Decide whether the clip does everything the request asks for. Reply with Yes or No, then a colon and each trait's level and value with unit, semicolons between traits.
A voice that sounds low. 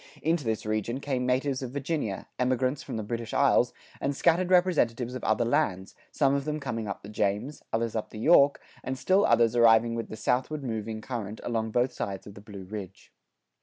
Yes: low, 120 Hz